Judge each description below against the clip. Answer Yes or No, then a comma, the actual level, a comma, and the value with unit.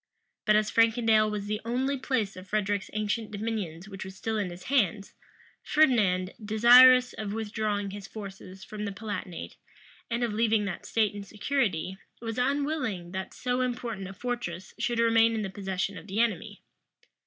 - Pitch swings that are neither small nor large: Yes, average, 3.0 semitones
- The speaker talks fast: No, average, 165 wpm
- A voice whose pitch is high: Yes, high, 215 Hz